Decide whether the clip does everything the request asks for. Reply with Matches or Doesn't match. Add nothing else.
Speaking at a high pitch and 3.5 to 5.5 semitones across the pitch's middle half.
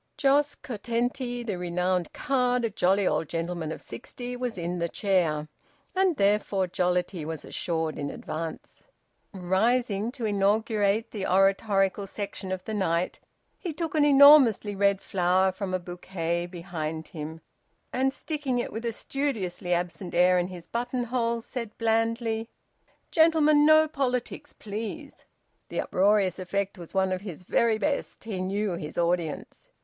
Matches